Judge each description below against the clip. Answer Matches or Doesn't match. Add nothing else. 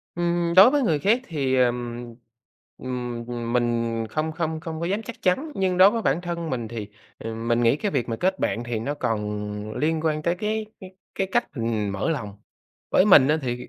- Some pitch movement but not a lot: Doesn't match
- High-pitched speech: Doesn't match